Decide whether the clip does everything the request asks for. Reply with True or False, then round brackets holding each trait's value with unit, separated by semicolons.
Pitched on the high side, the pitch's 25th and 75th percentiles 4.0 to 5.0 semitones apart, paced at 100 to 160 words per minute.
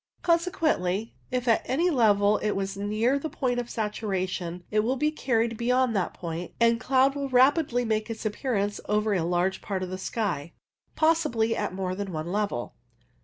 False (220 Hz; 4.7 semitones; 175 wpm)